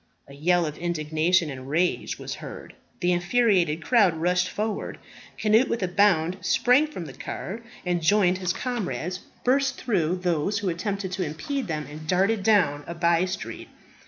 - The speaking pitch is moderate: Yes, medium, 180 Hz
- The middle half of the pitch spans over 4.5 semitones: No, average, 3.9 semitones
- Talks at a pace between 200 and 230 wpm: No, average, 165 wpm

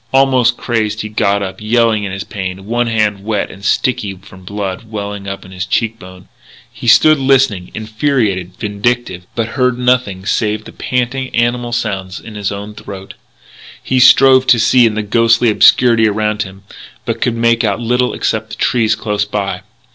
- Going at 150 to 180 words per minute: Yes, average, 175 wpm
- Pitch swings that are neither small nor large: Yes, average, 3.1 semitones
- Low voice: Yes, low, 110 Hz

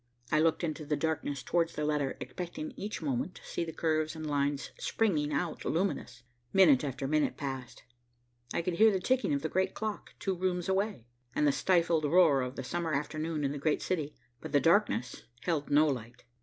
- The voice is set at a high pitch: No, medium, 155 Hz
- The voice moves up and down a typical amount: Yes, average, 3.8 semitones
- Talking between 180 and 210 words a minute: Yes, average, 195 wpm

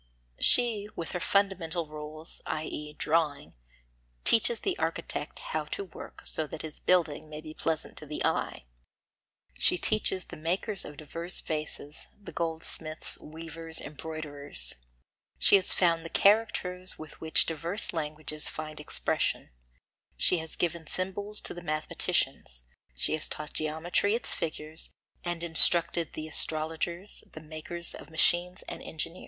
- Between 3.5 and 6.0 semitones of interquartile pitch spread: No, average, 2.7 semitones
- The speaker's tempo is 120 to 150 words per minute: Yes, average, 140 wpm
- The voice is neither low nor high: Yes, medium, 160 Hz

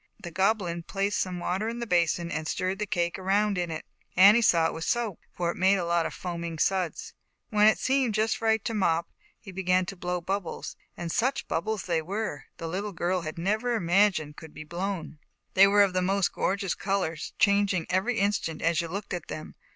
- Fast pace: Yes, fast, 220 wpm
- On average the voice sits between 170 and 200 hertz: Yes, medium, 185 Hz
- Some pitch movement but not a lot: Yes, average, 3.2 semitones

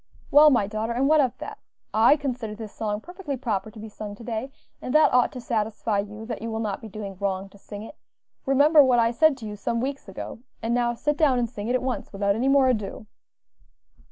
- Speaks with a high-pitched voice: Yes, high, 230 Hz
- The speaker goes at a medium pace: No, fast, 240 wpm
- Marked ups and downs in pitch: No, average, 3.9 semitones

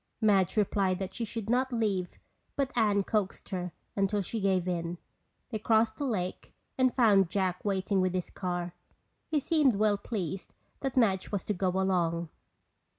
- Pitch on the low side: No, high, 200 Hz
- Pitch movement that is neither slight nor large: Yes, average, 3.3 semitones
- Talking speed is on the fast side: No, average, 165 wpm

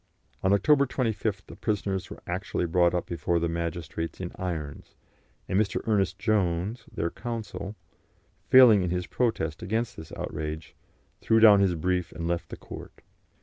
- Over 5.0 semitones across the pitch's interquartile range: No, average, 4.1 semitones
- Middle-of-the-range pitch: No, very low, 95 Hz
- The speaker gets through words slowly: No, average, 155 wpm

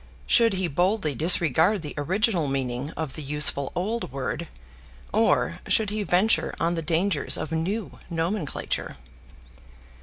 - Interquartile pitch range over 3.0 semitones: Yes, average, 5.1 semitones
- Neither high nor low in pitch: Yes, medium, 165 Hz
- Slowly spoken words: Yes, slow, 130 wpm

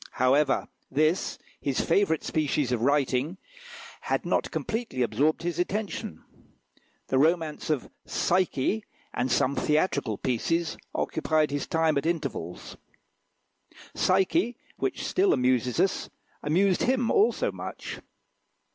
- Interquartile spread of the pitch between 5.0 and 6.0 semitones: Yes, wide, 5.6 semitones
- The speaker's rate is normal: No, slow, 110 wpm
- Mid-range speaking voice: Yes, medium, 155 Hz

